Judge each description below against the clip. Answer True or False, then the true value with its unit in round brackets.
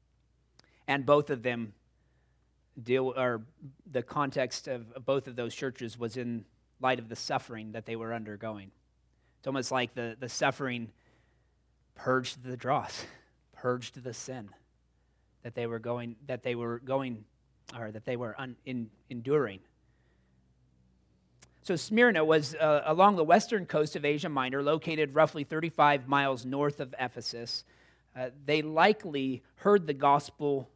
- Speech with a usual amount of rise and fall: True (3.9 semitones)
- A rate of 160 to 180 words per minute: False (145 wpm)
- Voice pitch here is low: True (125 Hz)